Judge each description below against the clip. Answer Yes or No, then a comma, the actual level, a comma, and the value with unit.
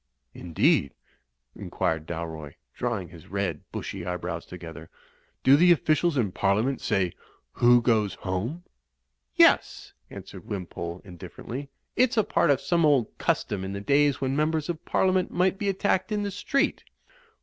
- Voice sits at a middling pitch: No, low, 120 Hz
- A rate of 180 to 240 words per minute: No, average, 150 wpm